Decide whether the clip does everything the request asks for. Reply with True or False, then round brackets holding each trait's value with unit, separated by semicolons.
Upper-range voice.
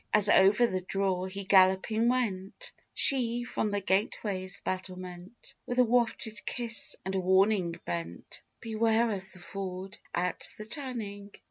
True (200 Hz)